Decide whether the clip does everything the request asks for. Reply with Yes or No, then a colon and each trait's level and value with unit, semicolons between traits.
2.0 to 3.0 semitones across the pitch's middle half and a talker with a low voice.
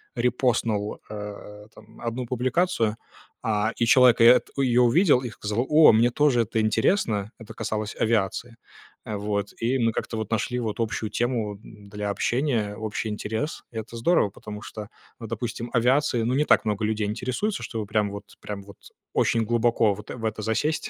Yes: average, 2.7 semitones; low, 115 Hz